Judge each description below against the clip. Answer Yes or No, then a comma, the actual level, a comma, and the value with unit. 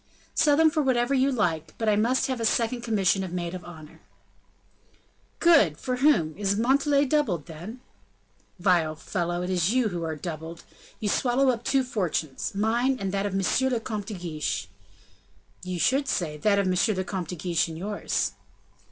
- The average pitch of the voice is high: Yes, high, 200 Hz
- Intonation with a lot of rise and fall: Yes, wide, 6.3 semitones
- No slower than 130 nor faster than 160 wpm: No, average, 185 wpm